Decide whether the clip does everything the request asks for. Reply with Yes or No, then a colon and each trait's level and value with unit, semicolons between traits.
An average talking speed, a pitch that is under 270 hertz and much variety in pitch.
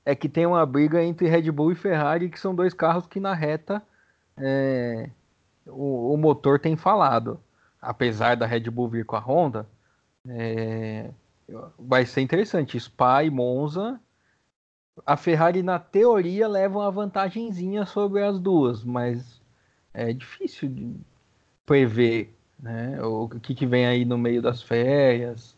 Yes: average, 150 wpm; medium, 140 Hz; wide, 6.5 semitones